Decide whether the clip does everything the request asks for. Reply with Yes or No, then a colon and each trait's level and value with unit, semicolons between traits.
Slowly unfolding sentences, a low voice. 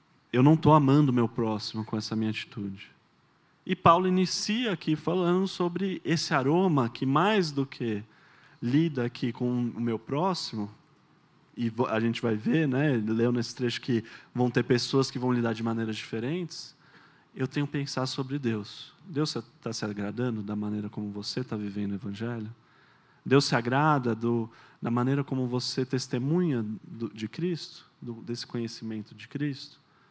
No: average, 165 wpm; low, 125 Hz